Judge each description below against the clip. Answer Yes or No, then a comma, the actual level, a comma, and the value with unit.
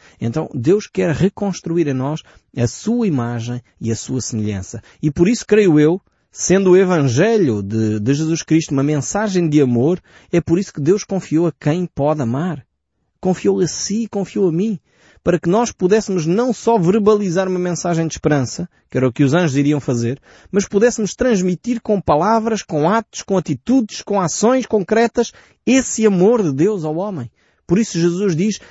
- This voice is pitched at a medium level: Yes, medium, 175 Hz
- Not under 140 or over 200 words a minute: Yes, average, 180 wpm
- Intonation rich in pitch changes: Yes, wide, 5.9 semitones